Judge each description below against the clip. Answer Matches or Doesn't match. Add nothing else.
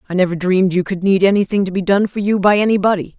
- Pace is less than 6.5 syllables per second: Doesn't match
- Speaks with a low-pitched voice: Doesn't match